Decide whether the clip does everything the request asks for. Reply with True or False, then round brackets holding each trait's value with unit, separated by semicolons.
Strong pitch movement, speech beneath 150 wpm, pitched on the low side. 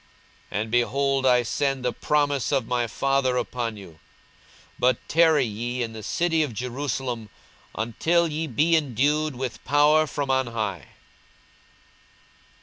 False (3.6 semitones; 140 wpm; 130 Hz)